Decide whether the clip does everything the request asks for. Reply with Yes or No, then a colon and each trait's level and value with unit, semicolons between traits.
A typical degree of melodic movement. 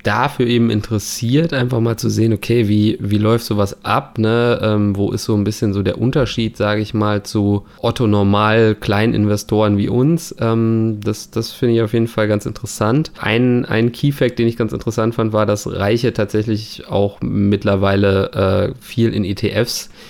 No: narrow, 2.0 semitones